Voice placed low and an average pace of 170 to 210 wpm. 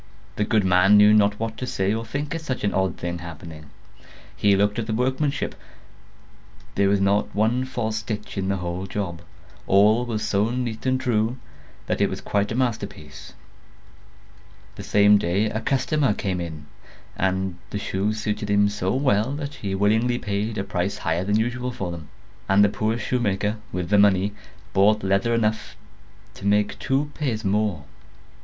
Yes: low, 105 Hz; average, 175 wpm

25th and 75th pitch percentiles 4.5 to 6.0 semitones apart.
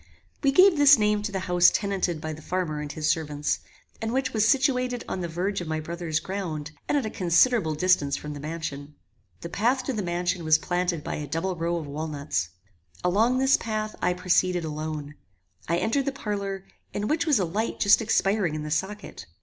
Yes: wide, 5.4 semitones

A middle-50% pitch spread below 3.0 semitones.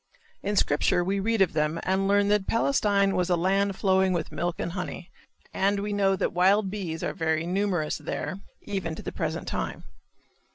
Yes: narrow, 2.5 semitones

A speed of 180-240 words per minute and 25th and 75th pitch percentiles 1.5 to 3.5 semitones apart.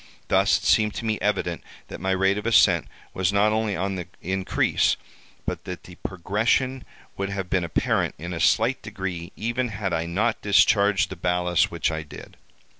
Yes: average, 185 wpm; average, 3.1 semitones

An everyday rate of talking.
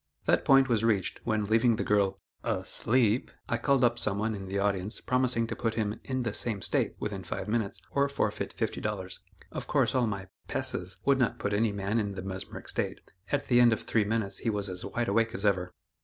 No: fast, 220 wpm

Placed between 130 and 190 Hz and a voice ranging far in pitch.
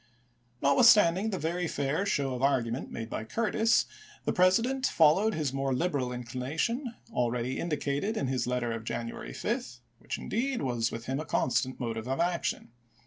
Yes: medium, 140 Hz; wide, 6.8 semitones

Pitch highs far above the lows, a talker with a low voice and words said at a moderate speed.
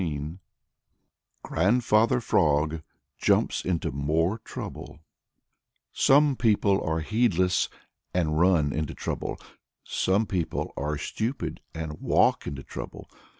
No: wide, 5.7 semitones; very low, 85 Hz; slow, 105 wpm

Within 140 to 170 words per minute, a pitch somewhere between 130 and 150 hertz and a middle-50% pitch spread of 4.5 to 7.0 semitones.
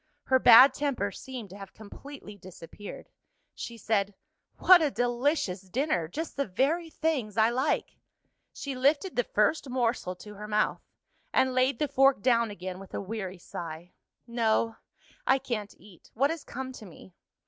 No: average, 160 wpm; high, 235 Hz; average, 5.0 semitones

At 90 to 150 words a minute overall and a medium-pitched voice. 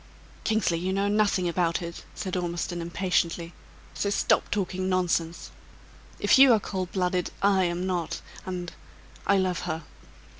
Yes: average, 145 wpm; medium, 180 Hz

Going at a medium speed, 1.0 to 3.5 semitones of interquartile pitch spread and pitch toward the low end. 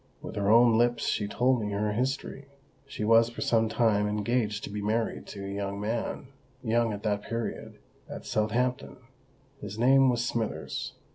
Yes: average, 160 wpm; narrow, 2.6 semitones; low, 115 Hz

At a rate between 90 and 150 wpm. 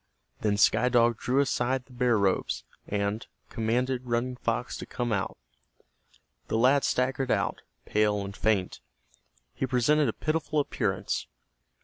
Yes: slow, 135 wpm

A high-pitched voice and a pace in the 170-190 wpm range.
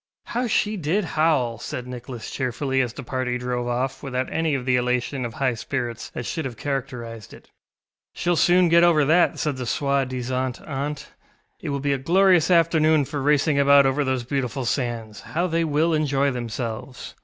No: low, 135 Hz; average, 185 wpm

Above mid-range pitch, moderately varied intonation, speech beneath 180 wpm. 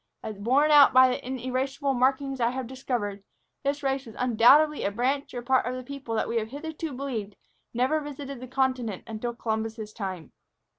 No: very high, 255 Hz; average, 3.2 semitones; average, 185 wpm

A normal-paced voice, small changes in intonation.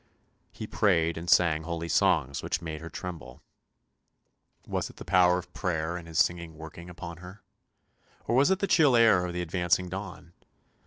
Yes: average, 175 wpm; narrow, 1.8 semitones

